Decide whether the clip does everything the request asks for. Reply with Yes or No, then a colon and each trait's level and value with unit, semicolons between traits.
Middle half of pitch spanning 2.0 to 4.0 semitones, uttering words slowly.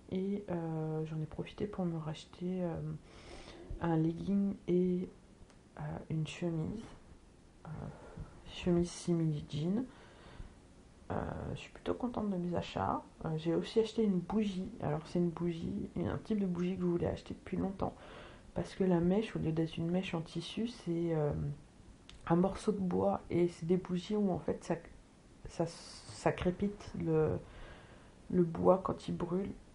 No: average, 2.8 semitones; average, 165 wpm